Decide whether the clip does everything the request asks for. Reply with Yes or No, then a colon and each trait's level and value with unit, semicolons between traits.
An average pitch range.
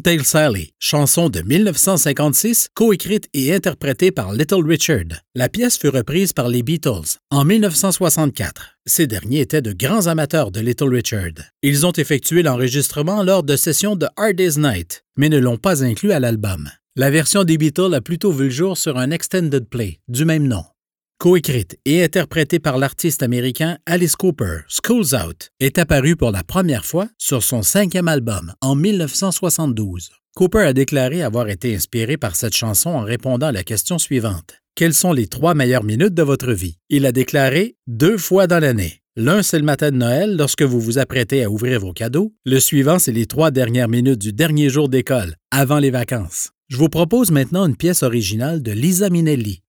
No: wide, 6.1 semitones